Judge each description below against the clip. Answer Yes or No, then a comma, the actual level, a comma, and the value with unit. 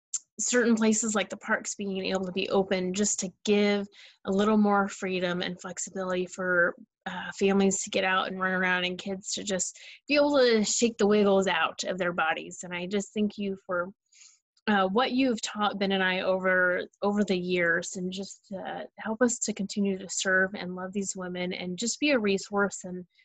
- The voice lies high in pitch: Yes, high, 195 Hz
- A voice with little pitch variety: Yes, narrow, 2.1 semitones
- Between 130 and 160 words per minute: No, average, 200 wpm